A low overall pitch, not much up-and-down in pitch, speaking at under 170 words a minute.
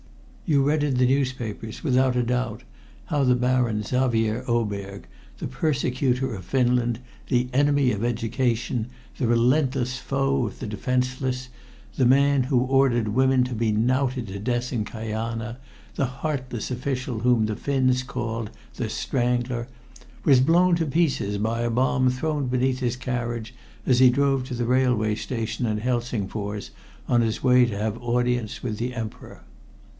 Yes: low, 125 Hz; narrow, 2.2 semitones; average, 155 wpm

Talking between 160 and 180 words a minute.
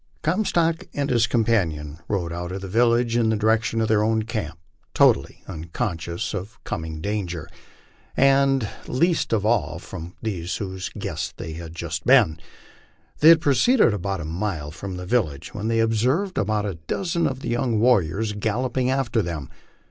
Yes: average, 170 wpm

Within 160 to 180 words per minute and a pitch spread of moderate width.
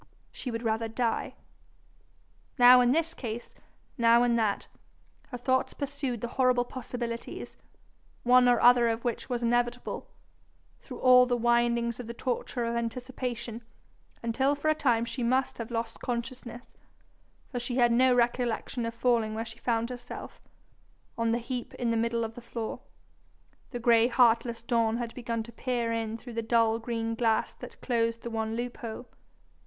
No: average, 165 wpm; narrow, 1.3 semitones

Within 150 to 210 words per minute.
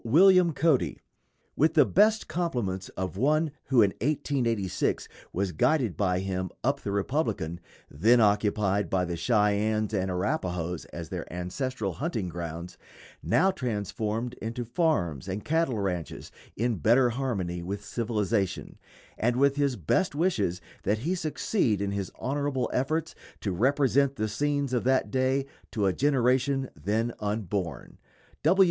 No: average, 140 wpm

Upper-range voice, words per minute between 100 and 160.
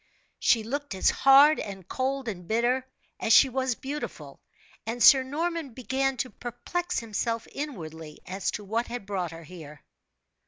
Yes: high, 240 Hz; average, 155 wpm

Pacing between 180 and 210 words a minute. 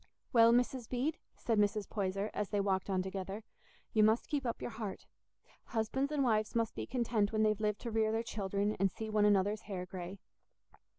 Yes: average, 195 wpm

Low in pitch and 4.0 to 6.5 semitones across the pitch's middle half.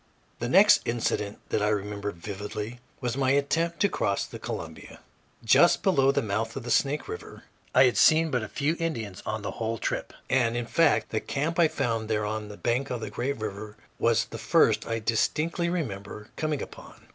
Yes: low, 120 Hz; average, 5.1 semitones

